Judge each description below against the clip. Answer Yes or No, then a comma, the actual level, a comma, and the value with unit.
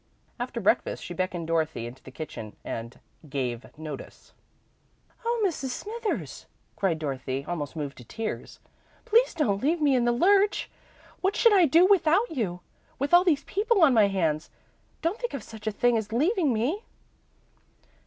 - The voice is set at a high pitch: Yes, high, 240 Hz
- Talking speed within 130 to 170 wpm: Yes, average, 165 wpm